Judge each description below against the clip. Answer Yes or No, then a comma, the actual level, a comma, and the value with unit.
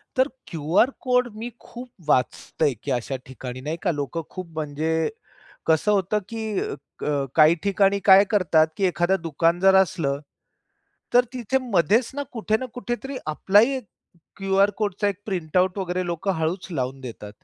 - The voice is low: No, medium, 185 Hz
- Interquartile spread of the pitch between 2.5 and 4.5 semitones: No, average, 5.0 semitones